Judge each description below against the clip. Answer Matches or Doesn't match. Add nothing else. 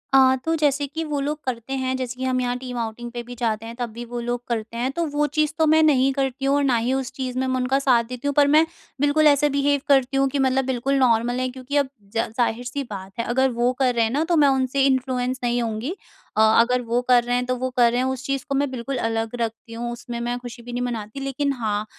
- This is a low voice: Doesn't match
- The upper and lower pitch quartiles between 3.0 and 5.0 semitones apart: Doesn't match